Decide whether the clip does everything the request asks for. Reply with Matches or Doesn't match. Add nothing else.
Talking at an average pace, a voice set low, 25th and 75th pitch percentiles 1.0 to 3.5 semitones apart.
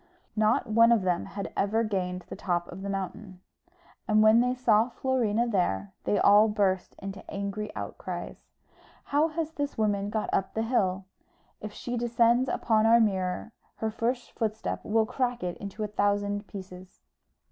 Doesn't match